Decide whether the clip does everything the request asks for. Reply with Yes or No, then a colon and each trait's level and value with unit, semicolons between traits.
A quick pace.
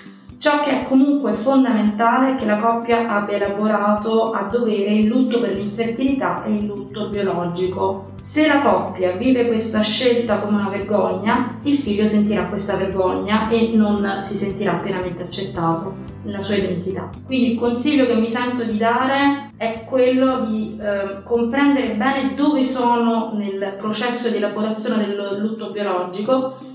No: average, 150 wpm